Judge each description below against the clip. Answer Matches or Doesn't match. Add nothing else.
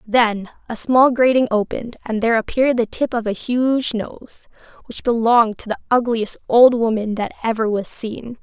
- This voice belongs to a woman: Matches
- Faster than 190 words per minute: Doesn't match